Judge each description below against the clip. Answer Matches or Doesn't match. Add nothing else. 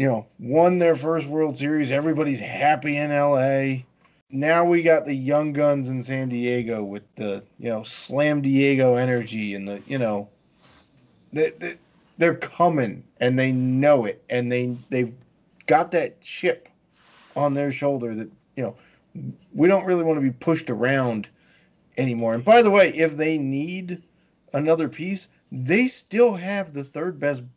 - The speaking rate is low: Doesn't match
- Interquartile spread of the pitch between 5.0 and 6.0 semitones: Doesn't match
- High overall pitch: Doesn't match